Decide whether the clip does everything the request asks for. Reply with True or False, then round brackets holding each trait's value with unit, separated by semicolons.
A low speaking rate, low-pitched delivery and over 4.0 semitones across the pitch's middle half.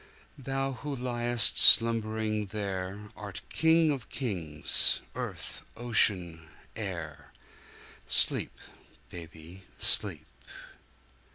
True (75 wpm; 105 Hz; 5.1 semitones)